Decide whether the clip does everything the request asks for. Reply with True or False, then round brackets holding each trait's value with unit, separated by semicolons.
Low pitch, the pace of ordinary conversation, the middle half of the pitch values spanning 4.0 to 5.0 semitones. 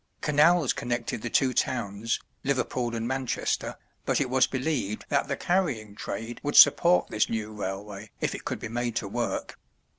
True (120 Hz; 170 wpm; 4.3 semitones)